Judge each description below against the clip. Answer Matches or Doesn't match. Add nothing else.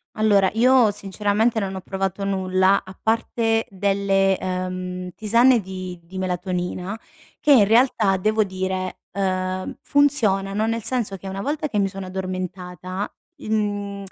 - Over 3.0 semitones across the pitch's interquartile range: Doesn't match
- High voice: Matches